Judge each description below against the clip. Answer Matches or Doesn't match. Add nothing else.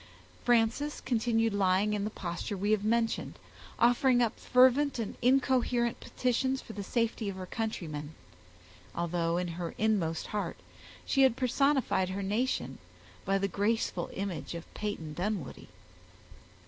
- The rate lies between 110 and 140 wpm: Matches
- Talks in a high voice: Matches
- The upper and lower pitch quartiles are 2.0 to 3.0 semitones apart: Doesn't match